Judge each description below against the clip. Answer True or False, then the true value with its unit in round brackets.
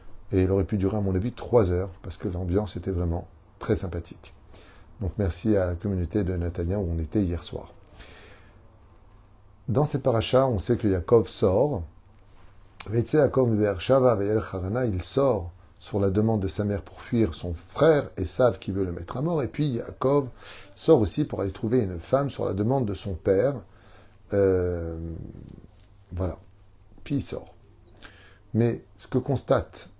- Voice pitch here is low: True (100 Hz)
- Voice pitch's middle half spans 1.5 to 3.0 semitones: False (3.4 semitones)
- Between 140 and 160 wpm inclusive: False (175 wpm)